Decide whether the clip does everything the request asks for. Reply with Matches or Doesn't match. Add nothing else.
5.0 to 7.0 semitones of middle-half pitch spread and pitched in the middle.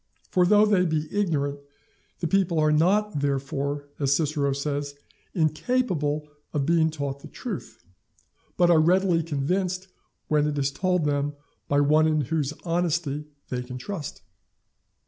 Doesn't match